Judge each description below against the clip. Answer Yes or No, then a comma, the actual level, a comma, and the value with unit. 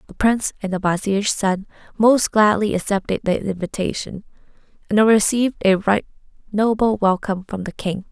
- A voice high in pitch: Yes, high, 205 Hz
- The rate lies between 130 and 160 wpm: Yes, average, 150 wpm